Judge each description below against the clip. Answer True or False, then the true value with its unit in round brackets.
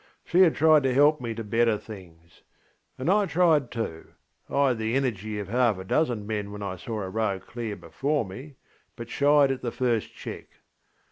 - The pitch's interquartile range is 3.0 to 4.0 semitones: False (5.4 semitones)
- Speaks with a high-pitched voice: False (115 Hz)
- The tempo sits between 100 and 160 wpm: False (190 wpm)